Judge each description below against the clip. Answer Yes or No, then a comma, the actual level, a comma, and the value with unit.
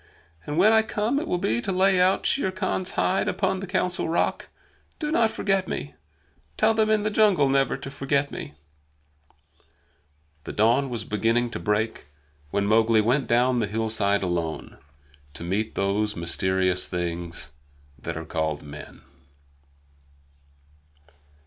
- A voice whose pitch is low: Yes, low, 120 Hz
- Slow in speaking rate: No, average, 145 wpm